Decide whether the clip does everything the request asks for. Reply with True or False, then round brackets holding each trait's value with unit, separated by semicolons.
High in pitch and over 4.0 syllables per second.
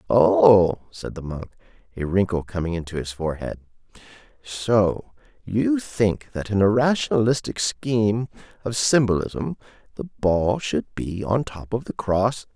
False (105 Hz; 4.2 syllables/s)